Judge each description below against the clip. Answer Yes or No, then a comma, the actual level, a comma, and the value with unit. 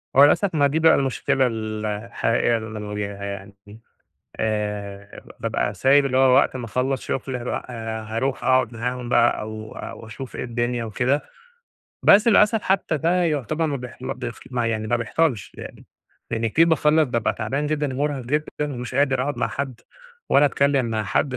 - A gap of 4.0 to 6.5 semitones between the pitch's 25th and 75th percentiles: Yes, average, 4.3 semitones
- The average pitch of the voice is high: No, low, 125 Hz